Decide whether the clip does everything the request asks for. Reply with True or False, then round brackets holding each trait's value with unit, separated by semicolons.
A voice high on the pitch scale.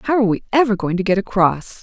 True (210 Hz)